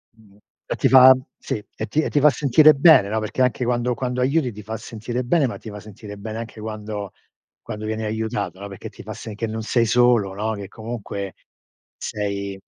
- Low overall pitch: Yes, low, 110 Hz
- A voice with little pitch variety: No, average, 3.0 semitones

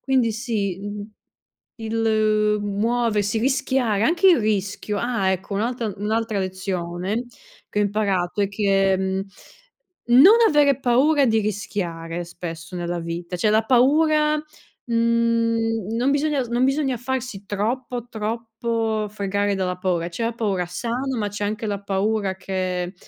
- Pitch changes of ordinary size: Yes, average, 3.5 semitones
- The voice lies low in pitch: No, high, 215 Hz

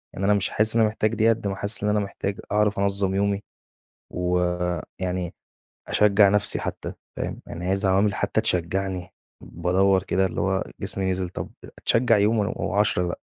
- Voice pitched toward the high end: No, low, 100 Hz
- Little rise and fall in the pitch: Yes, narrow, 1.9 semitones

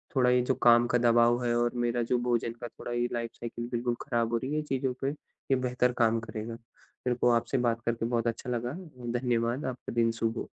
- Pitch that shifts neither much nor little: No, narrow, 1.1 semitones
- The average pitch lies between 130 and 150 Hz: No, low, 120 Hz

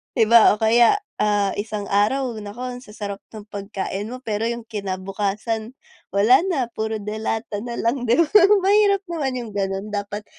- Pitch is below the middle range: No, high, 220 Hz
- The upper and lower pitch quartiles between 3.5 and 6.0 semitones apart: No, average, 2.9 semitones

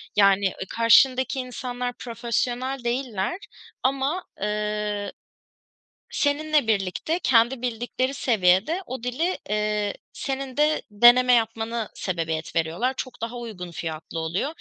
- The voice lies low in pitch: No, high, 235 Hz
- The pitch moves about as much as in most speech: Yes, average, 4.1 semitones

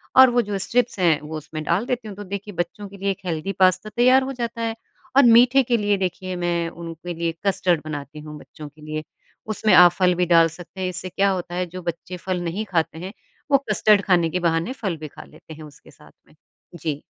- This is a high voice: No, medium, 180 Hz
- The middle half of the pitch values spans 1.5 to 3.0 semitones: No, average, 3.7 semitones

